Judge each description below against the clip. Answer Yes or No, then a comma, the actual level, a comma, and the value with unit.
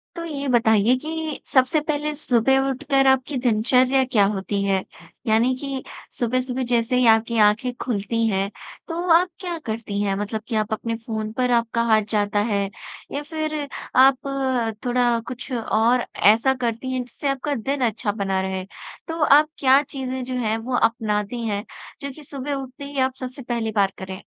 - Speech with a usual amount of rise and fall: Yes, average, 3.6 semitones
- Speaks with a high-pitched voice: Yes, high, 245 Hz